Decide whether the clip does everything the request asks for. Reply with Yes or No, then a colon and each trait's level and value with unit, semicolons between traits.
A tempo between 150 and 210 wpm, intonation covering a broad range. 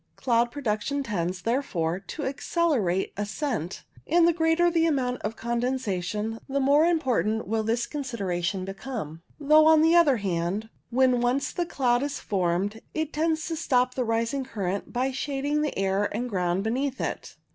Yes: average, 160 wpm; wide, 6.0 semitones